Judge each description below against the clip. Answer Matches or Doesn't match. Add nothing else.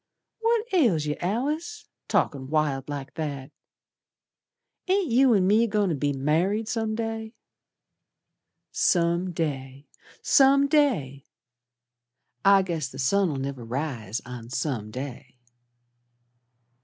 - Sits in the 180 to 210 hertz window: Doesn't match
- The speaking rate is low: Matches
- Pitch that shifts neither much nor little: Doesn't match